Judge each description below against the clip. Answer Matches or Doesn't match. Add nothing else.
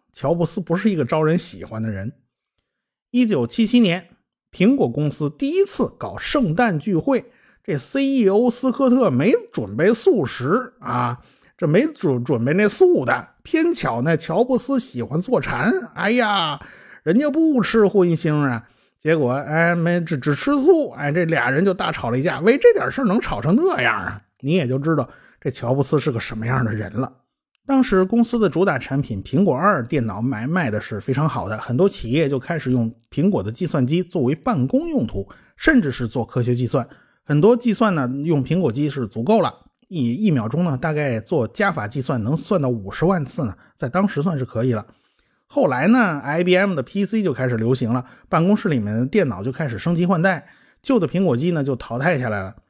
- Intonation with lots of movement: Matches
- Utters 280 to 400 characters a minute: Matches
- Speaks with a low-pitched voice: Doesn't match